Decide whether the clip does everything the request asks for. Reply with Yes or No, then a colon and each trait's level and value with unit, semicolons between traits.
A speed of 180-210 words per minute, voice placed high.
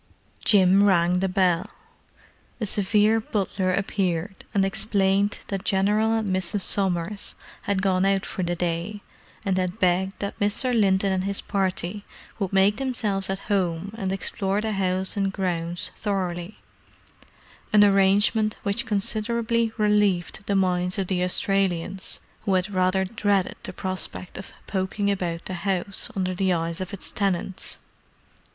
No: average, 145 wpm; high, 195 Hz